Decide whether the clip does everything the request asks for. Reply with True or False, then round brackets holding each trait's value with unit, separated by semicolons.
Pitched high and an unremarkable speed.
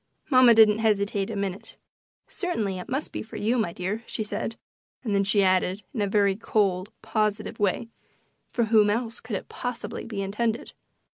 True (210 Hz; 180 wpm)